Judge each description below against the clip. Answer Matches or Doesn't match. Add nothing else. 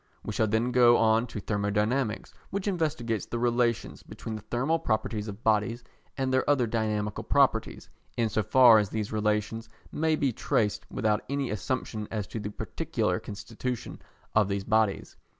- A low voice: Matches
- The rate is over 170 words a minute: Doesn't match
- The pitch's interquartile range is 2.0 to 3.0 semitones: Matches